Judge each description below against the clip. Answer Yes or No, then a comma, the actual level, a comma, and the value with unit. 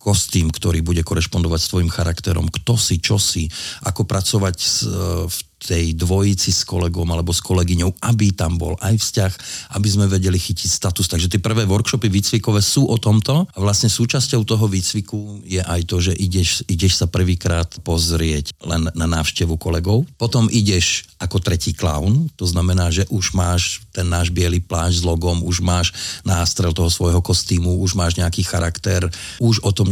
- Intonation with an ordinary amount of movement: Yes, average, 3.1 semitones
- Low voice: Yes, very low, 95 Hz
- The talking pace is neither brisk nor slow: No, fast, 175 wpm